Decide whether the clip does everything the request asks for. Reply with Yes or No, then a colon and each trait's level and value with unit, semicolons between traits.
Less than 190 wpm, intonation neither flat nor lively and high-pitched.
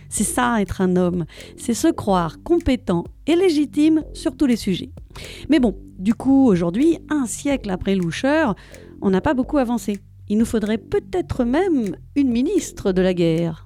No: average, 170 wpm; wide, 8.1 semitones; high, 235 Hz